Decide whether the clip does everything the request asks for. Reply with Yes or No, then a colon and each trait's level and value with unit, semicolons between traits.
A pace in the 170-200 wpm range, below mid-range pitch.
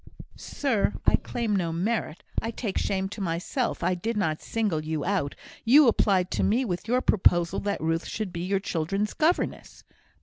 No: average, 175 wpm; high, 195 Hz